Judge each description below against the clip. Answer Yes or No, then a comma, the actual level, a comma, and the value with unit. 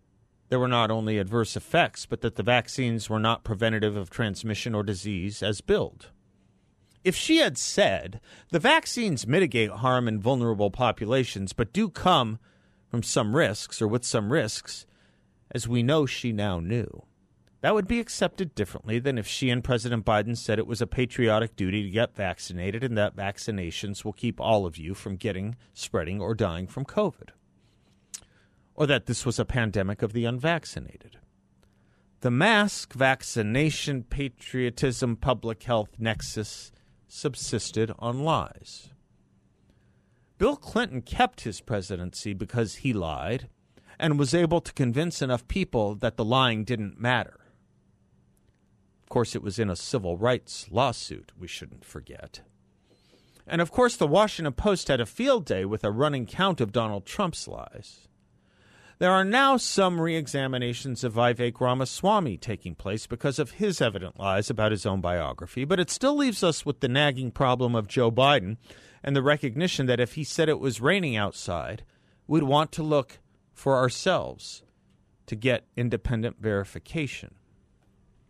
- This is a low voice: Yes, low, 120 Hz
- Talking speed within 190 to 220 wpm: No, average, 155 wpm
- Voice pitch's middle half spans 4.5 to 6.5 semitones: Yes, average, 4.9 semitones